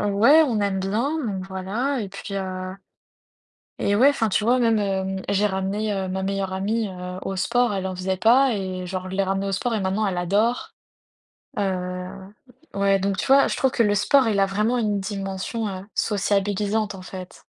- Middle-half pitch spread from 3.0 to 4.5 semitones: No, narrow, 2.5 semitones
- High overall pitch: Yes, high, 200 Hz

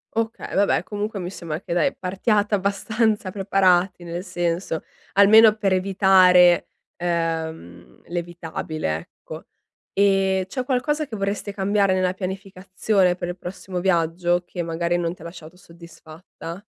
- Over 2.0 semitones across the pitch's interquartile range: Yes, narrow, 2.6 semitones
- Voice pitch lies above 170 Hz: Yes, medium, 185 Hz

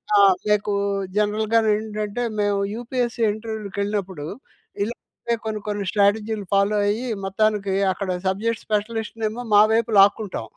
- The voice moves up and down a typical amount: No, narrow, 1.5 semitones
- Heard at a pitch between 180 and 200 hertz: No, high, 210 Hz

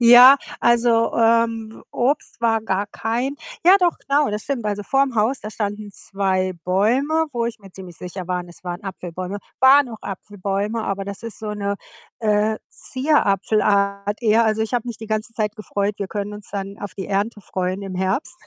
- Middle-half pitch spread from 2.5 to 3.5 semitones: Yes, average, 2.8 semitones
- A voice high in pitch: Yes, high, 210 Hz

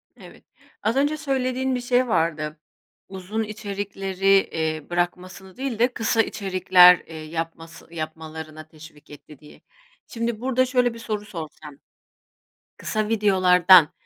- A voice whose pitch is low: No, high, 190 Hz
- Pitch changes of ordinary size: No, wide, 5.8 semitones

